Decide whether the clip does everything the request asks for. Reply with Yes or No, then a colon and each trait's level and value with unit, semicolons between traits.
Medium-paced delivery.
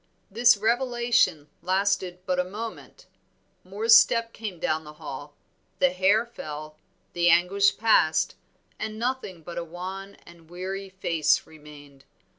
No: slow, 130 wpm